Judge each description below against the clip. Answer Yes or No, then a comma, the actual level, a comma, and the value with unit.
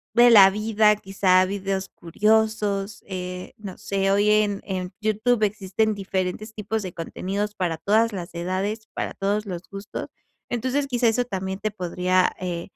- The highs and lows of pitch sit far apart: No, narrow, 2.5 semitones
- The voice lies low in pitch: No, high, 200 Hz